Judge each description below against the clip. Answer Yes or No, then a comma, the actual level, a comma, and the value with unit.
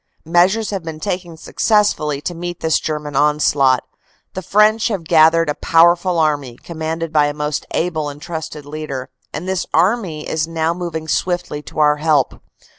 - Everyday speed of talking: Yes, average, 170 wpm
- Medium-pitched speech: Yes, medium, 160 Hz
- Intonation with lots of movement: No, average, 2.8 semitones